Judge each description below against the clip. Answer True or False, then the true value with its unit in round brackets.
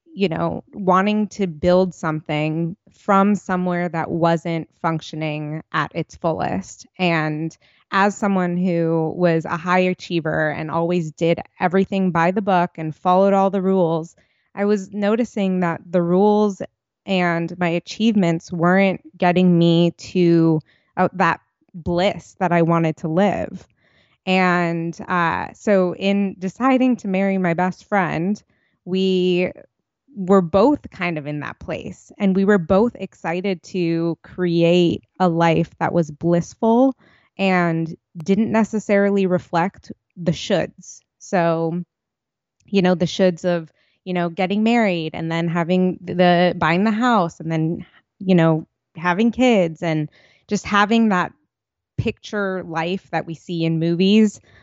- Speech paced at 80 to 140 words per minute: True (135 wpm)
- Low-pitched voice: False (180 Hz)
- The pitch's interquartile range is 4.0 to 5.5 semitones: False (2.7 semitones)